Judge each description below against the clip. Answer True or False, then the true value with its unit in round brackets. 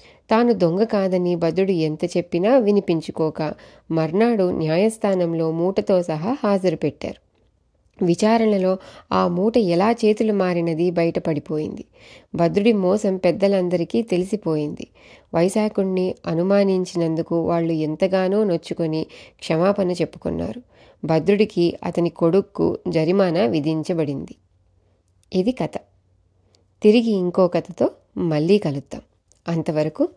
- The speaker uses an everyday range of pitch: True (3.8 semitones)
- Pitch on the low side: False (175 Hz)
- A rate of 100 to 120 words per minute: False (90 wpm)